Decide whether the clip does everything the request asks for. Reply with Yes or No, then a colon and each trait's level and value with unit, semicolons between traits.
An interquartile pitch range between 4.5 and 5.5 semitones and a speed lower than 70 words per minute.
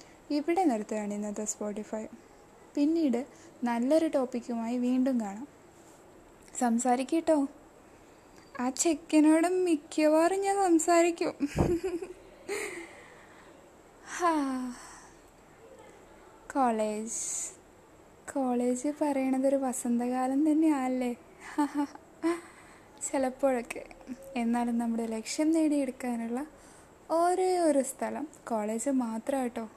Yes: average, 4.8 semitones; slow, 60 wpm